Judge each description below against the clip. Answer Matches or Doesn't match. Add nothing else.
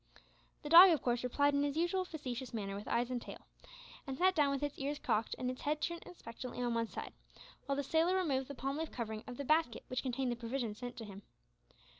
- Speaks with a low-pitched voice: Doesn't match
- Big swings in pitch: Doesn't match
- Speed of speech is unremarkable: Doesn't match